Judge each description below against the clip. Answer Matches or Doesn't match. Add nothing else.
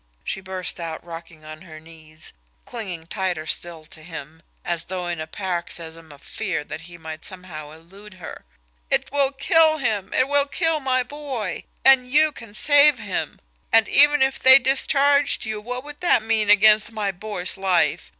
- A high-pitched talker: Matches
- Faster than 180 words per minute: Doesn't match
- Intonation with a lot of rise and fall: Matches